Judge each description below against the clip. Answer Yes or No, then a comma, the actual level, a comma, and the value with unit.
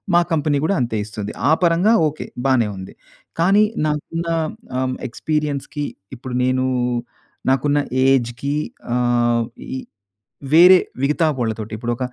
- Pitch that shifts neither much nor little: Yes, average, 4.4 semitones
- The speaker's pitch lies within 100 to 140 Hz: Yes, low, 135 Hz